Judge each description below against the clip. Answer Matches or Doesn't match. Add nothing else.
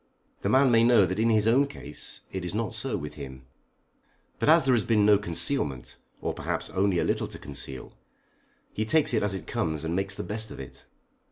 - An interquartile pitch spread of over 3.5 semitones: Matches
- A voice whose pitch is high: Doesn't match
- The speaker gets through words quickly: Matches